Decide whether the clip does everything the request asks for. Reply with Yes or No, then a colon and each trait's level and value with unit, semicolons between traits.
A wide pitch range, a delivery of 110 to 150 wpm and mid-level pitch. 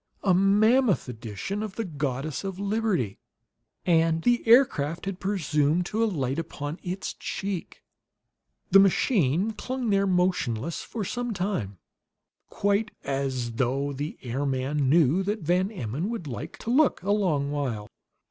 Yes: wide, 6.5 semitones; average, 140 wpm; medium, 175 Hz